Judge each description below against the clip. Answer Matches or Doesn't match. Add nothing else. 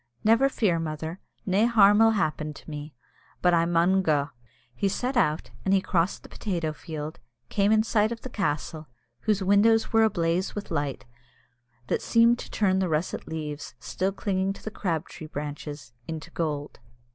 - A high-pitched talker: Doesn't match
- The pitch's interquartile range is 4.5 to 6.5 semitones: Matches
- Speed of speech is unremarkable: Matches